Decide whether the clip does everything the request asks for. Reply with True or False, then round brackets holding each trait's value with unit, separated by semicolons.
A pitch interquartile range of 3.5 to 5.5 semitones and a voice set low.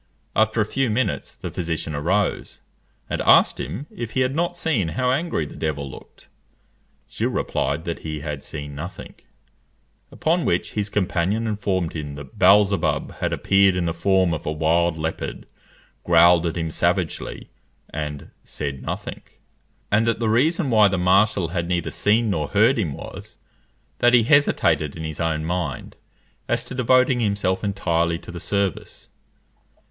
True (5.2 semitones; 95 Hz)